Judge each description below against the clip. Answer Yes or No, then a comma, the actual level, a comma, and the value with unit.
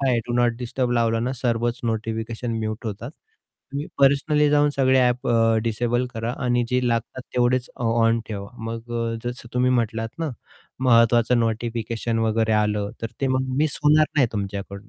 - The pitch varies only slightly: Yes, narrow, 2.0 semitones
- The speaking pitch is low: Yes, low, 120 Hz